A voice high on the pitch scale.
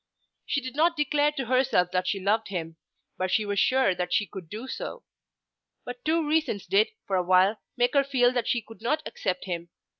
Yes: high, 235 Hz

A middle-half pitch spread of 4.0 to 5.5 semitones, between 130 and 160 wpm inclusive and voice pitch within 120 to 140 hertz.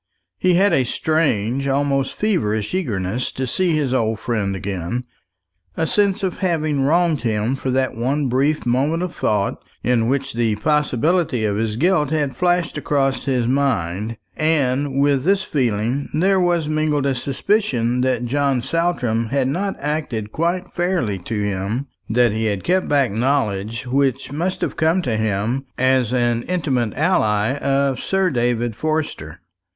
Yes: average, 5.2 semitones; average, 155 wpm; low, 135 Hz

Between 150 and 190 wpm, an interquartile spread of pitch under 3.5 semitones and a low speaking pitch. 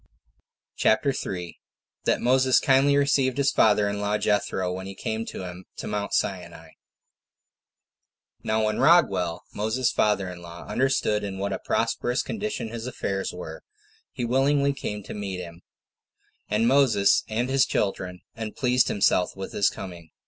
No: average, 155 wpm; average, 5.2 semitones; low, 105 Hz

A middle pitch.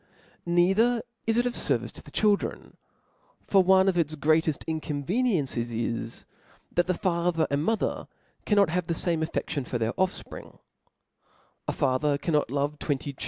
Yes: medium, 165 Hz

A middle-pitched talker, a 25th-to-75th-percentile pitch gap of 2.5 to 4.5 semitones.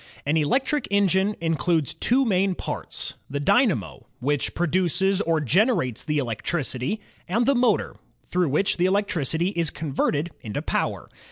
No: medium, 175 Hz; wide, 5.4 semitones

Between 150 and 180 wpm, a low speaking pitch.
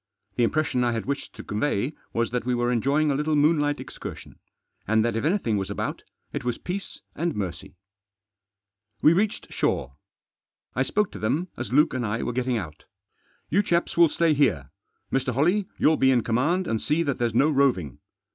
No: average, 195 wpm; low, 130 Hz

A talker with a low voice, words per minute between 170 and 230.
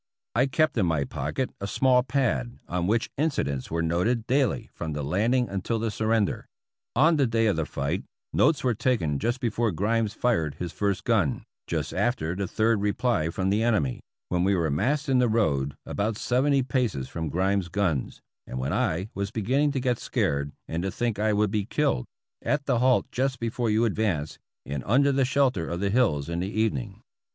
Yes: low, 105 Hz; average, 200 wpm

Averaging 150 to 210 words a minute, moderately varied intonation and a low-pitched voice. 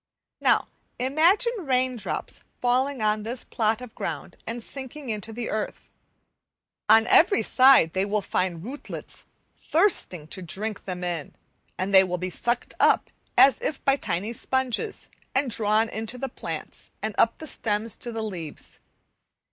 No: average, 155 wpm; average, 4.3 semitones; high, 225 Hz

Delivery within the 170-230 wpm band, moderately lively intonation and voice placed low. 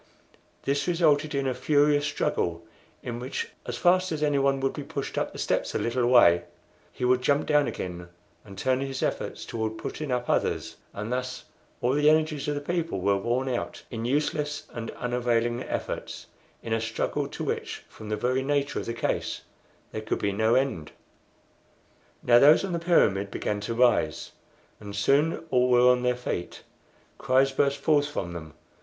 Yes: average, 180 wpm; average, 4.1 semitones; low, 125 Hz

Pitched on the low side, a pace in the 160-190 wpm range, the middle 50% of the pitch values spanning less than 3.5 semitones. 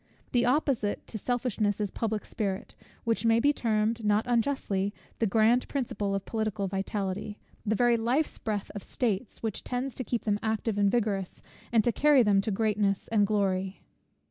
No: high, 215 Hz; average, 170 wpm; average, 2.8 semitones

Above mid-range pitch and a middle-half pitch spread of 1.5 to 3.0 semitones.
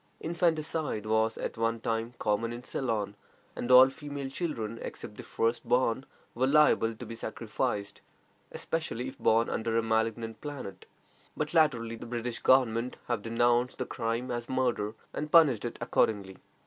No: low, 120 Hz; average, 2.7 semitones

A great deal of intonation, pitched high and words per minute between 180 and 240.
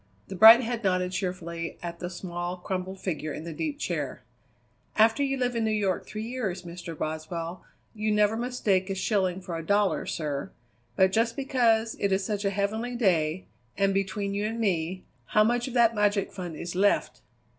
No: average, 3.9 semitones; high, 195 Hz; average, 190 wpm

